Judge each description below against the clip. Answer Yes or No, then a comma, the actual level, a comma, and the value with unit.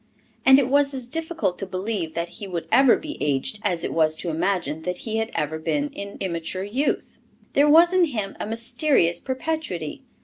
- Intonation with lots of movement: Yes, wide, 8.4 semitones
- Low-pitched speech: No, high, 205 Hz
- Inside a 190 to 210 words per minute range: Yes, average, 195 wpm